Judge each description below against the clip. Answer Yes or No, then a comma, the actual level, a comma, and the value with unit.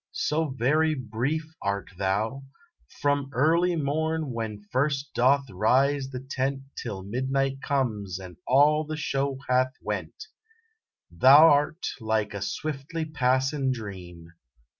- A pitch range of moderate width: Yes, average, 4.8 semitones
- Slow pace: Yes, slow, 120 wpm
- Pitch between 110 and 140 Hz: Yes, low, 135 Hz